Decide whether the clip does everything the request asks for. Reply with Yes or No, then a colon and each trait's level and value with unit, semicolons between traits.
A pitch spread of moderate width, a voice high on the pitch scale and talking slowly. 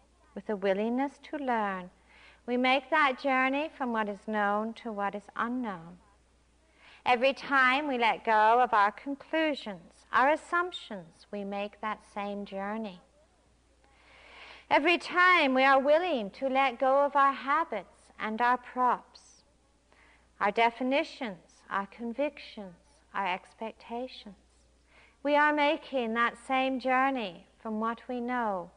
Yes: average, 4.9 semitones; high, 245 Hz; slow, 130 wpm